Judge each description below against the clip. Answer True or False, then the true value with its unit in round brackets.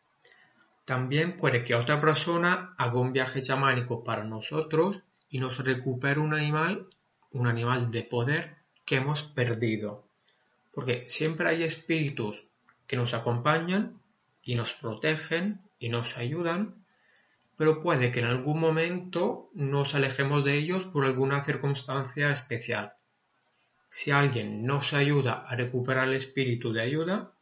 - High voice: False (140 Hz)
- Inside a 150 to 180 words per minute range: False (130 wpm)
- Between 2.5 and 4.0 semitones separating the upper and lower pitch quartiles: False (4.4 semitones)